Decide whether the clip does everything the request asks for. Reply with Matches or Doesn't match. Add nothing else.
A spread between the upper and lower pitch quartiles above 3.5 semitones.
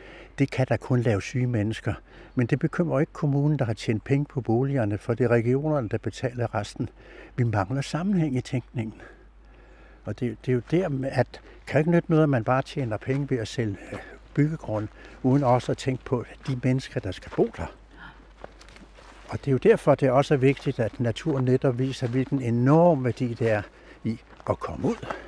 Doesn't match